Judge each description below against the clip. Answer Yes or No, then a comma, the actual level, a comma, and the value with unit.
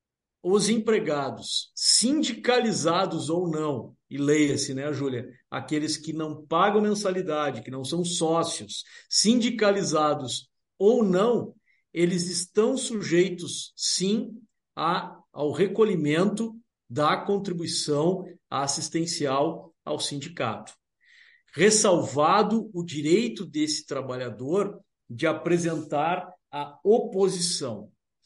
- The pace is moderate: No, slow, 90 wpm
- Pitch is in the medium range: Yes, medium, 175 Hz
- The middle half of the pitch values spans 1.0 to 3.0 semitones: No, wide, 5.4 semitones